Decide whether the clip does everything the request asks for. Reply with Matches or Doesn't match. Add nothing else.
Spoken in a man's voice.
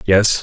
Matches